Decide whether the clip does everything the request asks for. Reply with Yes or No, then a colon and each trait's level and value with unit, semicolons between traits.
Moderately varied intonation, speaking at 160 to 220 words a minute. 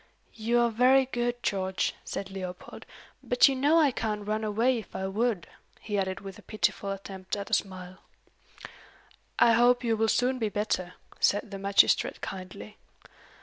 Yes: average, 3.8 semitones; average, 165 wpm